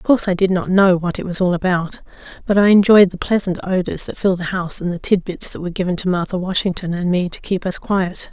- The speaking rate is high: Yes, fast, 260 wpm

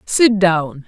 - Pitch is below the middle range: No, high, 190 Hz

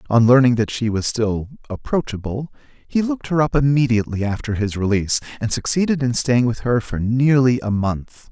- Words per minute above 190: No, average, 180 wpm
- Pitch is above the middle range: No, low, 120 Hz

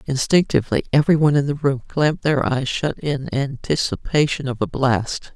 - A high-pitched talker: No, medium, 140 Hz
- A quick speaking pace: No, average, 155 wpm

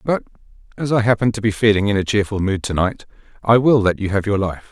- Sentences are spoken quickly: Yes, fast, 255 wpm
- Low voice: Yes, low, 105 Hz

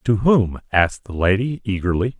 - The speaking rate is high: No, average, 165 wpm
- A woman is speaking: No, male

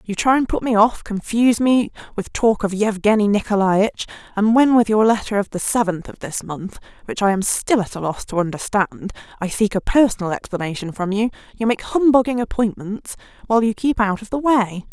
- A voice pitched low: No, high, 215 Hz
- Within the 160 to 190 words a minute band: No, fast, 205 wpm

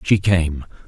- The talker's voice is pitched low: Yes, very low, 85 Hz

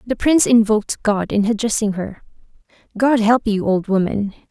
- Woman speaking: Yes, female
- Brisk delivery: No, average, 160 wpm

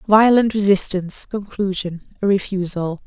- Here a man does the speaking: No, female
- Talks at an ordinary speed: No, slow, 100 wpm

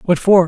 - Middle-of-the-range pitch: Yes, medium, 180 Hz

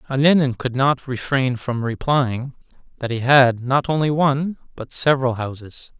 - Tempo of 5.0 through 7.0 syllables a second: No, 4.7 syllables/s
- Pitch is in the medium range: No, low, 130 Hz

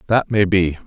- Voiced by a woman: No, male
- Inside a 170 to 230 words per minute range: Yes, fast, 210 wpm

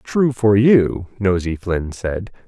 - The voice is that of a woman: No, male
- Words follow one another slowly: No, average, 145 wpm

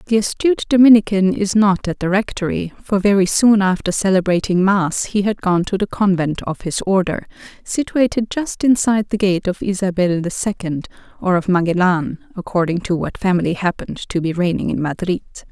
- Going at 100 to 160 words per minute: No, average, 175 wpm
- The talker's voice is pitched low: No, high, 190 Hz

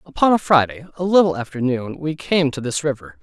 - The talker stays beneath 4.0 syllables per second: No, 5.8 syllables/s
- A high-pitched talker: No, medium, 145 Hz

